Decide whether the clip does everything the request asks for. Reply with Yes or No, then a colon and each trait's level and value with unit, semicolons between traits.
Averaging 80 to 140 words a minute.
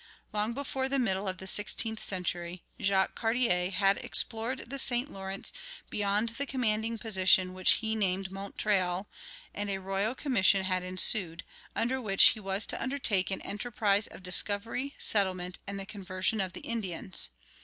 No: average, 155 wpm